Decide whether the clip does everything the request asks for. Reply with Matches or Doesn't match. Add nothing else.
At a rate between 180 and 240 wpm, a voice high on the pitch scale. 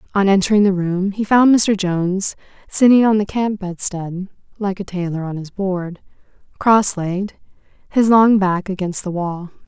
Doesn't match